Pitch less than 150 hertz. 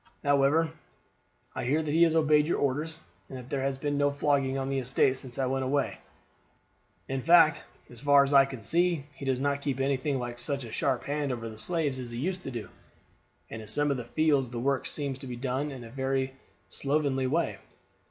Yes: low, 135 Hz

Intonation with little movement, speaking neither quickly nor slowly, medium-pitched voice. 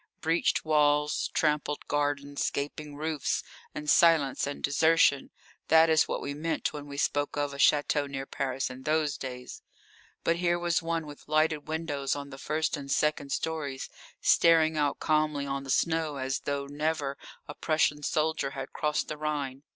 Yes: narrow, 1.9 semitones; average, 165 wpm; medium, 150 Hz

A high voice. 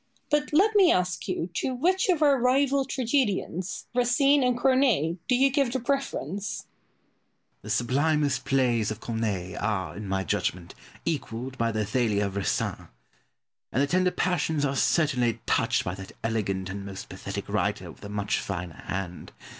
No: medium, 145 Hz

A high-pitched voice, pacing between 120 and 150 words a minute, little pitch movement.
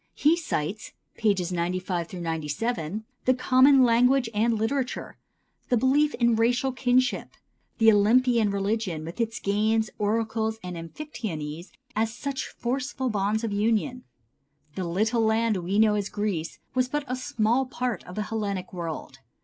No: high, 220 Hz; average, 140 wpm; average, 4.2 semitones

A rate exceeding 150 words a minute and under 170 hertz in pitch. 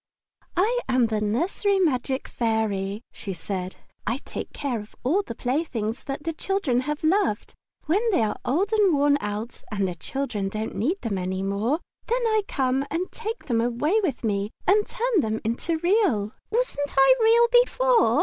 No: average, 175 wpm; very high, 270 Hz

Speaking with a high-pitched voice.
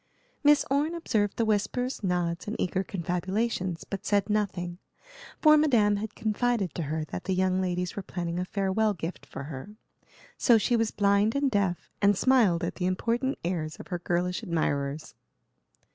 Yes: high, 195 Hz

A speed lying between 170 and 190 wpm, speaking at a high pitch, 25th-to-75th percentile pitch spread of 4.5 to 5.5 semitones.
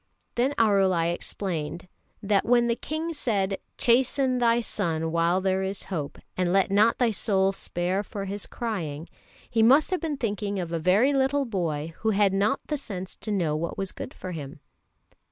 Yes: average, 180 wpm; high, 195 Hz; average, 4.9 semitones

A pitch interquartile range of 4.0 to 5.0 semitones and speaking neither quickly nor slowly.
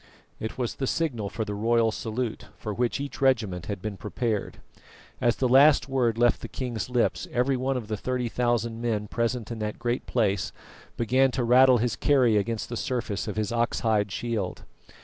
No: average, 2.7 semitones; average, 190 wpm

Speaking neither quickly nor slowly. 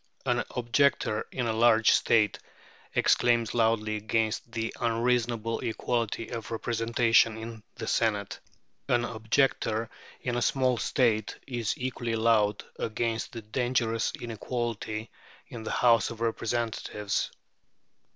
No: slow, 115 wpm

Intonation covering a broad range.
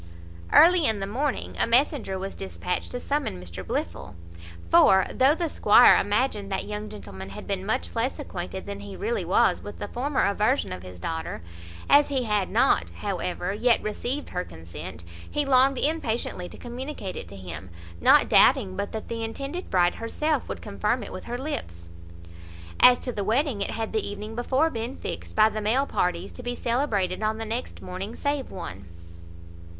Yes: wide, 5.8 semitones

